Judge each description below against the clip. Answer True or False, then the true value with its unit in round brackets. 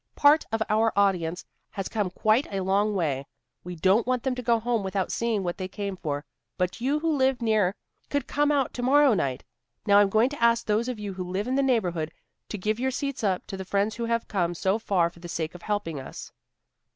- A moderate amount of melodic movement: True (4.6 semitones)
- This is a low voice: False (210 Hz)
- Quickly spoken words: True (235 wpm)